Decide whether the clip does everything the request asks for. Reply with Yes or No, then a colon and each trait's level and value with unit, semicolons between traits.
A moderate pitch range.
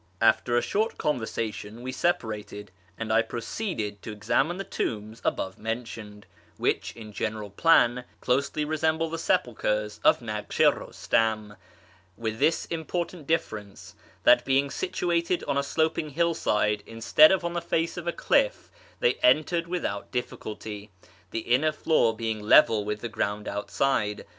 No: wide, 7.0 semitones